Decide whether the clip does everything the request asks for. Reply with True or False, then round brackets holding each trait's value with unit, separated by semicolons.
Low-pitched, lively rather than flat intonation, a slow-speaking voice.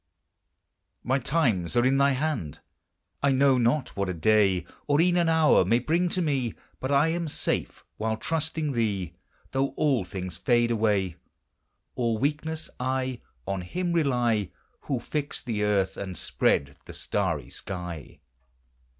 False (125 Hz; 6.7 semitones; 150 wpm)